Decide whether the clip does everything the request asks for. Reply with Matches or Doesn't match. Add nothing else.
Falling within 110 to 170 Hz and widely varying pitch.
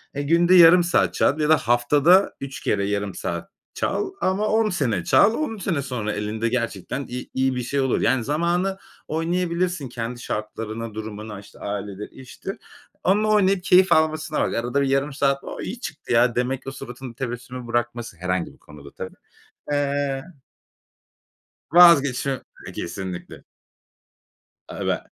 Matches